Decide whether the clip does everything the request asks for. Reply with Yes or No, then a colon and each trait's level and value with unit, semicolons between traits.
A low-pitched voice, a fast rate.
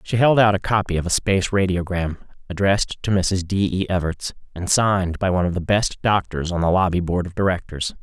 Yes: very low, 95 Hz; fast, 215 wpm